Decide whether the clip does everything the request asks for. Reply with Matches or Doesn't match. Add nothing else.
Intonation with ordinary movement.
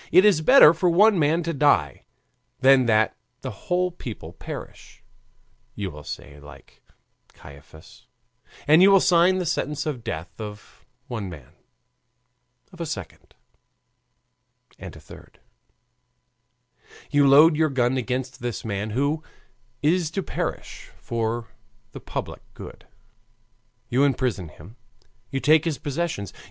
Doesn't match